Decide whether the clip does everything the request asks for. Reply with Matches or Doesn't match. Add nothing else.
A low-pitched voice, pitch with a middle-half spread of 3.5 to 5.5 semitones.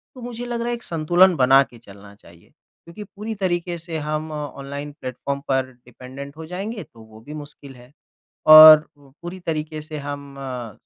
Doesn't match